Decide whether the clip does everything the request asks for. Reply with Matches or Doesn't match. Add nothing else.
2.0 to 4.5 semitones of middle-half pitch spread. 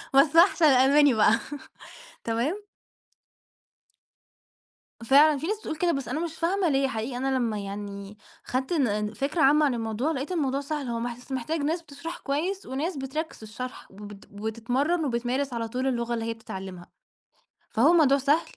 Doesn't match